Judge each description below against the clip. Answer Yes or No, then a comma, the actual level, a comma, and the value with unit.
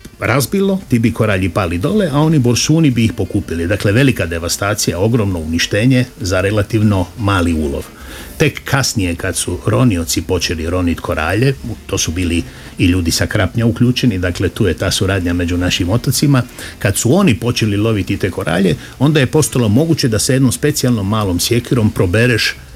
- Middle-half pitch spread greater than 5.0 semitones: Yes, wide, 5.5 semitones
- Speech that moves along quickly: Yes, fast, 165 wpm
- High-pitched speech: No, low, 105 Hz